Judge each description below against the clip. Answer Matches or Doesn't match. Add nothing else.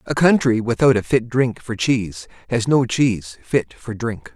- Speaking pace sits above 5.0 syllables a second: Doesn't match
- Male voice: Matches